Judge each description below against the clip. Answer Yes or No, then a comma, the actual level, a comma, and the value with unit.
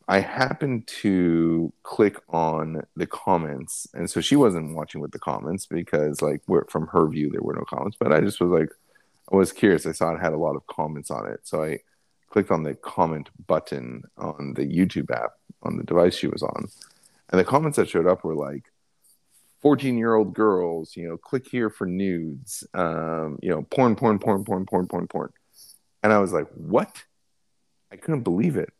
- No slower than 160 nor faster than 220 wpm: Yes, average, 200 wpm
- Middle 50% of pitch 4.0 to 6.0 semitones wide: Yes, wide, 5.6 semitones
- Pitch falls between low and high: No, very low, 90 Hz